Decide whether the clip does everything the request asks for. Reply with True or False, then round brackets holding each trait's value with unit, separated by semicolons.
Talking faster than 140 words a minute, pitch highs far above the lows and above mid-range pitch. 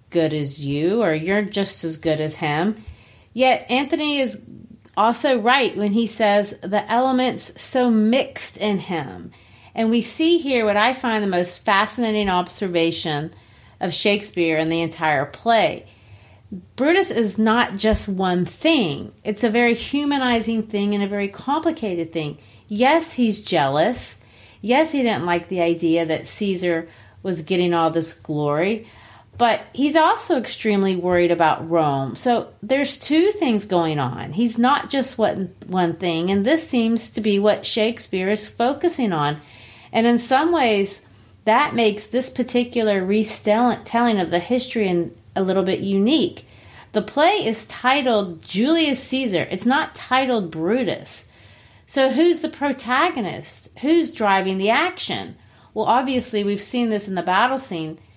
True (150 wpm; 6.1 semitones; 210 Hz)